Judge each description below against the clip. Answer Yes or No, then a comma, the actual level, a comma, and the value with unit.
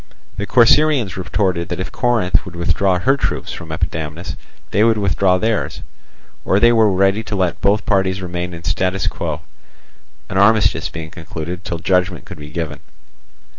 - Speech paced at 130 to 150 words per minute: No, average, 165 wpm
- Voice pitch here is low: Yes, very low, 95 Hz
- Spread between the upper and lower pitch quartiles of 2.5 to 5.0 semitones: Yes, average, 3.3 semitones